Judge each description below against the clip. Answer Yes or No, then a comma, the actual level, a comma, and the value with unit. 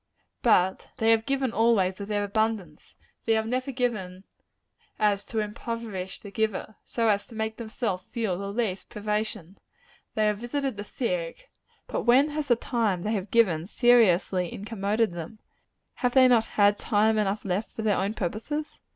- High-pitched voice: Yes, high, 215 Hz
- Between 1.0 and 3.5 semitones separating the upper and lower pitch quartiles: Yes, average, 2.8 semitones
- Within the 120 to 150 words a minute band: No, average, 170 wpm